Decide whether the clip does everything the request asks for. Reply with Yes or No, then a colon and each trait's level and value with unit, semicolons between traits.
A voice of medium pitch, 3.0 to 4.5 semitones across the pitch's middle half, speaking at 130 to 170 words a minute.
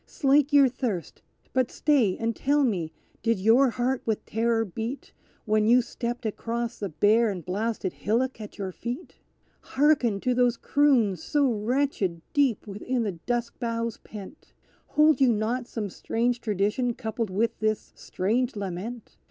No: high, 230 Hz; average, 3.3 semitones; average, 150 wpm